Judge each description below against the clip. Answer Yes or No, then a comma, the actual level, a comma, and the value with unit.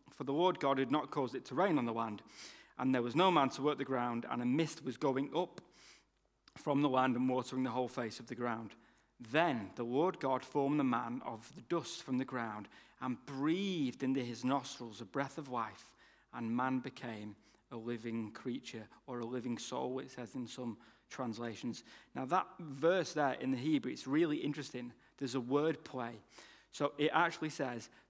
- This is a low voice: Yes, low, 130 Hz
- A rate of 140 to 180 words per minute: No, average, 200 wpm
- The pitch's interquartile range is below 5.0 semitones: Yes, average, 3.3 semitones